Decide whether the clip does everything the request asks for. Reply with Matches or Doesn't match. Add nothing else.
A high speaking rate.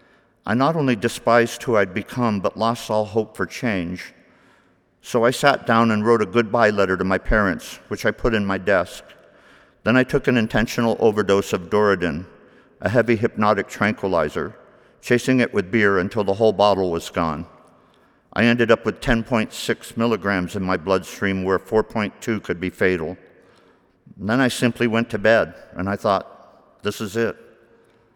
Doesn't match